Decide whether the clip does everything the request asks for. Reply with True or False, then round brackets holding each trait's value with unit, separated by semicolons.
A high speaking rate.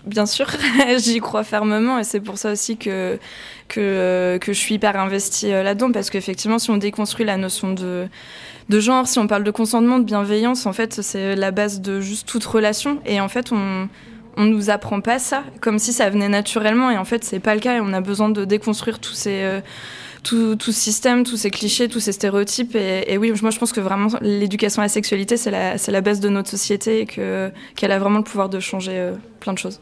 True (230 wpm)